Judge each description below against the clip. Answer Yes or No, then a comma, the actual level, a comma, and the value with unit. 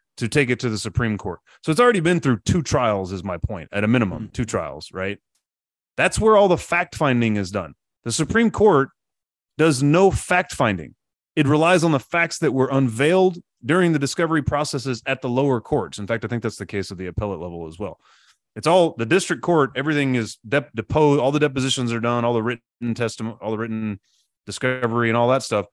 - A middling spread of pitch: No, wide, 5.7 semitones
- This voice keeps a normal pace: No, fast, 215 wpm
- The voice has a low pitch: Yes, low, 125 Hz